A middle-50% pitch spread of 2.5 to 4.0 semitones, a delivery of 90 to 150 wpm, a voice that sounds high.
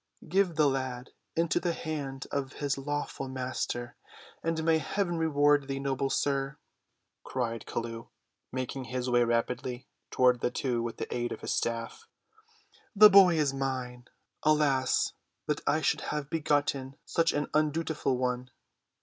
No: average, 3.4 semitones; average, 140 wpm; low, 135 Hz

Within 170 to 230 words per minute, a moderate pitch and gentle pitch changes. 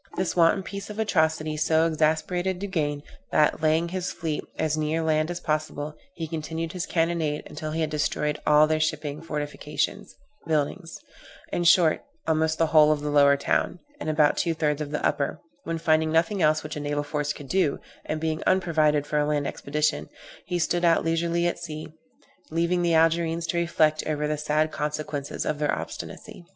Yes: average, 185 wpm; medium, 155 Hz; narrow, 1.7 semitones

